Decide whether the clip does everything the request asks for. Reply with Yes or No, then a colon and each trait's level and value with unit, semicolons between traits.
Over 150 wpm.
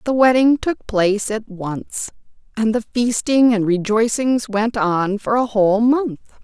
Yes: average, 160 wpm